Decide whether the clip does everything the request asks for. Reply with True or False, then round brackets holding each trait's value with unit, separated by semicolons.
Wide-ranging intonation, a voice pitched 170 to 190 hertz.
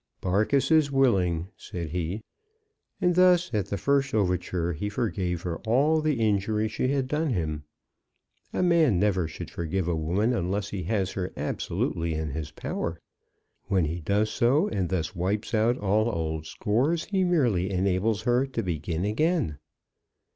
False (6.1 semitones; 100 Hz)